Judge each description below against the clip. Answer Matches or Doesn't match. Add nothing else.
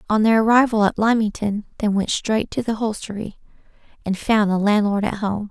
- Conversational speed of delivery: Matches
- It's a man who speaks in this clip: Doesn't match